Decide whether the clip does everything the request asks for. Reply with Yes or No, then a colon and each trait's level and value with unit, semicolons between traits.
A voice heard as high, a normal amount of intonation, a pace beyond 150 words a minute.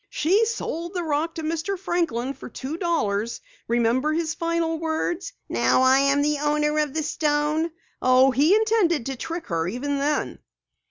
Yes: very high, 305 Hz; average, 3.7 semitones; average, 165 wpm